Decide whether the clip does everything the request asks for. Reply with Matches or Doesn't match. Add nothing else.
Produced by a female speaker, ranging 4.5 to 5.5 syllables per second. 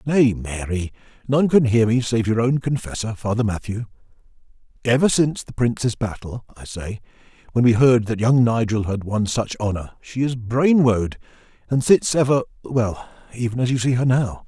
Doesn't match